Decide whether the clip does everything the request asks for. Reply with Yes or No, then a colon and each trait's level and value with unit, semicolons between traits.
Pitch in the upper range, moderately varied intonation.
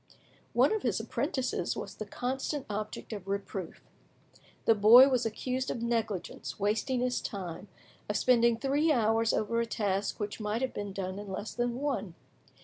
Yes: high, 225 Hz; average, 3.6 semitones